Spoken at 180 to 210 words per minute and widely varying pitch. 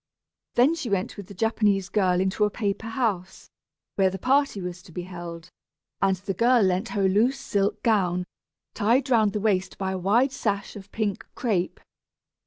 No: average, 185 wpm; average, 3.2 semitones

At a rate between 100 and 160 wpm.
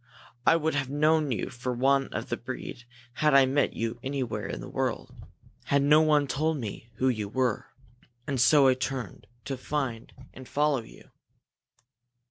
No: average, 175 wpm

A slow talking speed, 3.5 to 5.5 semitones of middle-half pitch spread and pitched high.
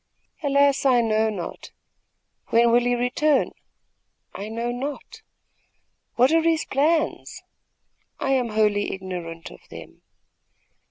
Yes: slow, 115 wpm; average, 4.7 semitones; high, 245 Hz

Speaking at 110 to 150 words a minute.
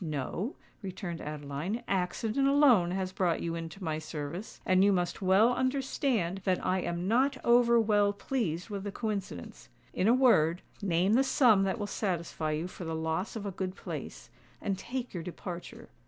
No: average, 170 wpm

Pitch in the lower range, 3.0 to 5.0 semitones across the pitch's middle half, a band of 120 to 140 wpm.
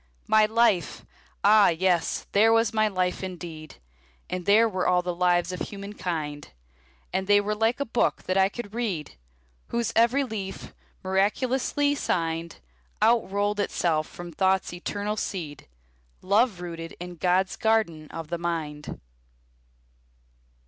No: high, 190 Hz; average, 3.9 semitones; slow, 135 wpm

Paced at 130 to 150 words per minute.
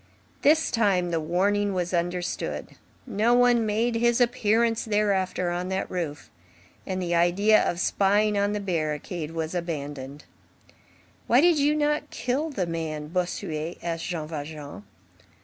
Yes: average, 140 wpm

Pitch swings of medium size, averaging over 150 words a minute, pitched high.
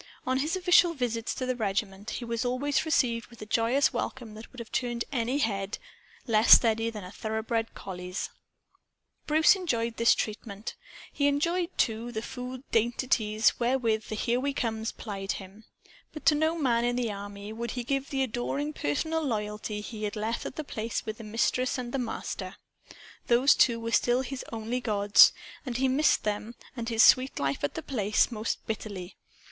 Yes: average, 3.2 semitones; average, 185 wpm; high, 230 Hz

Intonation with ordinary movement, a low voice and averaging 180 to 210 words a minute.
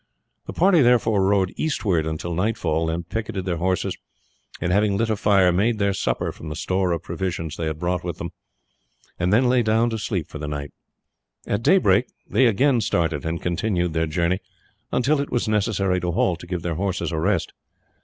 Yes: average, 4.3 semitones; very low, 95 Hz; average, 195 wpm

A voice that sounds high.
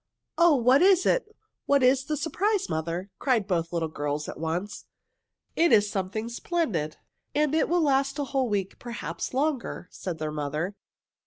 Yes: high, 235 Hz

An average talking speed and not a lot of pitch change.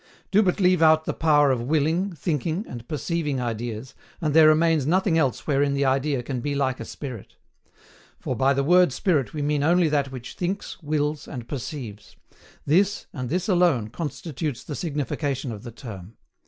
No: average, 180 wpm; average, 4.0 semitones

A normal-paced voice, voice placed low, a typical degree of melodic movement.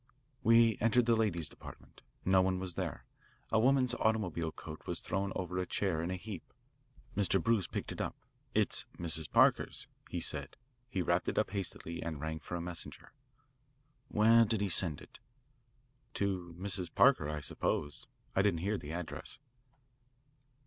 Yes: average, 165 wpm; very low, 95 Hz; average, 4.3 semitones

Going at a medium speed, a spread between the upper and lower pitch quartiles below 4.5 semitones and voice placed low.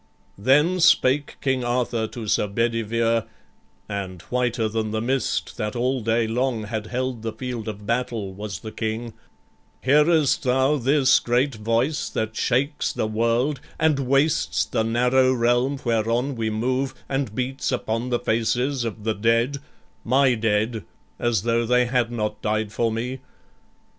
Yes: average, 150 wpm; average, 2.8 semitones; low, 120 Hz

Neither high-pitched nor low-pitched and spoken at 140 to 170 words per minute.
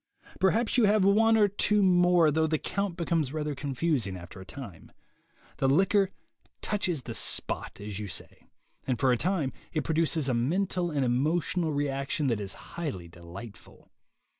Yes: medium, 155 Hz; average, 165 wpm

